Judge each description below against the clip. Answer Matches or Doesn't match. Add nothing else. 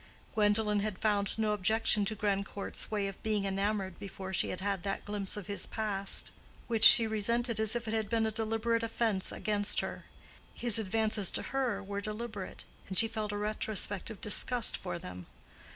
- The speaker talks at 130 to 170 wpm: Doesn't match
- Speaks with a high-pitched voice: Matches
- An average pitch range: Doesn't match